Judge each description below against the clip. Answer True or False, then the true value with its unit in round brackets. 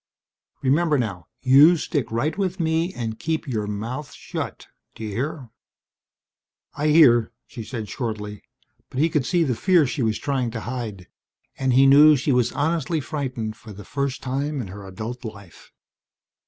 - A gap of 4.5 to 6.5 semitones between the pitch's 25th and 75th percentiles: True (5.2 semitones)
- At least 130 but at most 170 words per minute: True (165 wpm)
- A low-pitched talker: True (130 Hz)